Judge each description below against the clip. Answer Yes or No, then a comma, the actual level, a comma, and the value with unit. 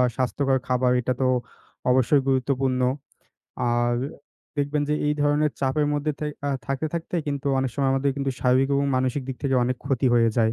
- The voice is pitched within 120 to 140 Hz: Yes, low, 135 Hz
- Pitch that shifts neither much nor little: No, narrow, 2.0 semitones